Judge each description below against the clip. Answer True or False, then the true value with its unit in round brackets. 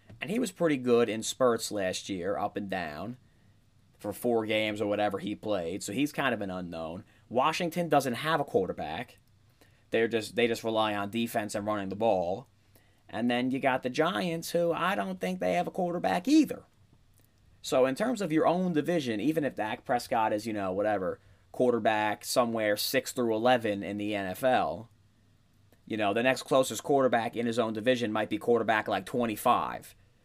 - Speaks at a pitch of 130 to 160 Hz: False (115 Hz)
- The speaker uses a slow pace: False (190 wpm)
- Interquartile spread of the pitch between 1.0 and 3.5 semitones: False (4.0 semitones)